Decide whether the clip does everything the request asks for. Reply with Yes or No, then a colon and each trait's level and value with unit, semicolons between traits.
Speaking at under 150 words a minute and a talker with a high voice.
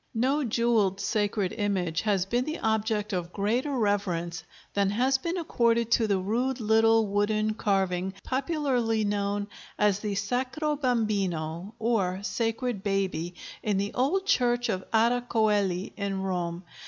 Yes: average, 140 wpm; high, 215 Hz